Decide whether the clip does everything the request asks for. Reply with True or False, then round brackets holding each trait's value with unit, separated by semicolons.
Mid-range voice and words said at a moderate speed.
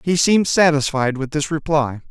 True (150 Hz; 170 wpm)